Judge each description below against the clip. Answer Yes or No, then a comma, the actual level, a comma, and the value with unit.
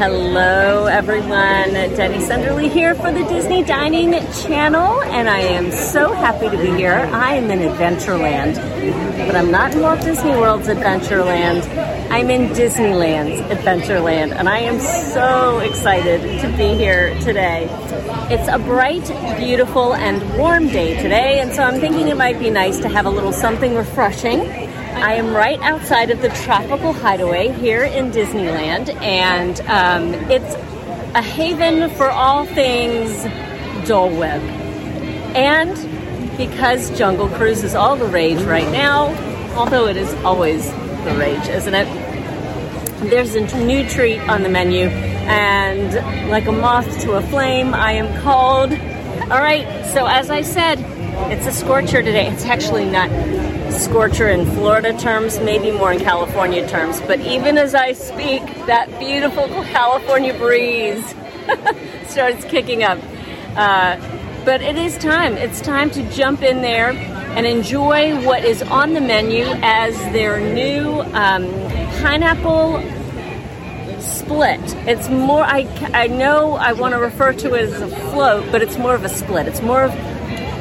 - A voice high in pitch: Yes, high, 240 Hz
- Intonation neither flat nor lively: No, wide, 5.9 semitones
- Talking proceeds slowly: No, average, 150 wpm